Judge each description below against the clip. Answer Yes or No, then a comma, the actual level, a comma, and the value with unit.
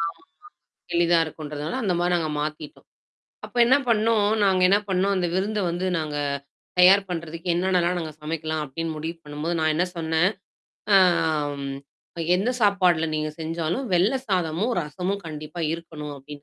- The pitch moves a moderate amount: Yes, average, 3.1 semitones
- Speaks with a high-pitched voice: No, medium, 170 Hz